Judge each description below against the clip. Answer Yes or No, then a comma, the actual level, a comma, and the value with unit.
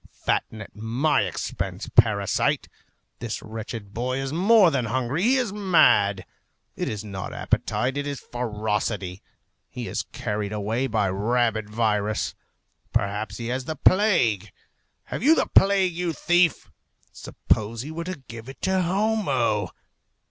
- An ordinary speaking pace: Yes, average, 145 wpm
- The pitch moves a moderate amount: No, wide, 7.7 semitones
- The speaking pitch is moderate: No, low, 120 Hz